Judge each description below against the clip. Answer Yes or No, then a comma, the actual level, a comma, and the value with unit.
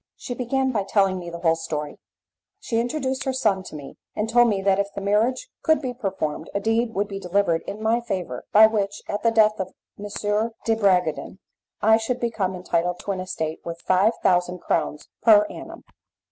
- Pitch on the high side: Yes, high, 205 Hz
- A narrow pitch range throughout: No, average, 3.8 semitones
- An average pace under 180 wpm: No, average, 200 wpm